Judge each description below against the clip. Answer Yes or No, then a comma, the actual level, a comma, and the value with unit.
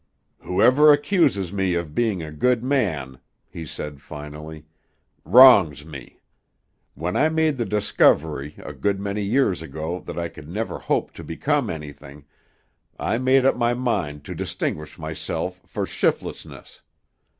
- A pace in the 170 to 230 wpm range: No, average, 140 wpm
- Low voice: Yes, very low, 95 Hz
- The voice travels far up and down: Yes, wide, 8.3 semitones